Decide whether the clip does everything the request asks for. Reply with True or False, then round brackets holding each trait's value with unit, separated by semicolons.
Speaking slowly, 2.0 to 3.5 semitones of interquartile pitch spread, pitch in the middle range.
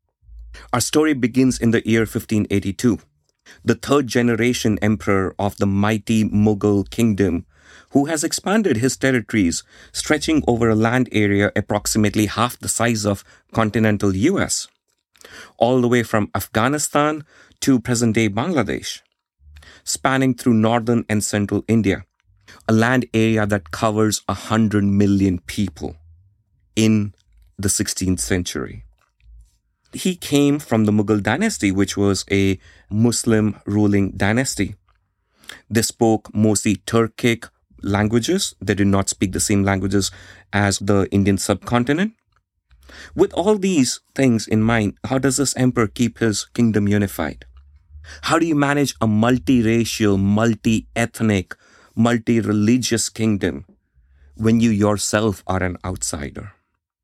False (125 wpm; 3.1 semitones; 105 Hz)